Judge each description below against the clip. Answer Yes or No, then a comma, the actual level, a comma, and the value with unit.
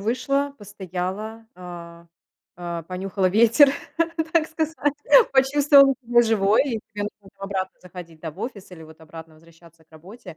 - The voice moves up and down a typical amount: No, wide, 5.9 semitones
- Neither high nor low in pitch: No, high, 195 Hz